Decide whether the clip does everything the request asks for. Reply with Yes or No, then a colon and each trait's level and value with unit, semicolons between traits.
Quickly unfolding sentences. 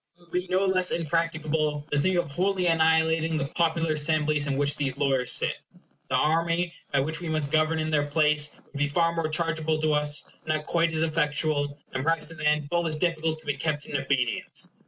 Yes: fast, 215 wpm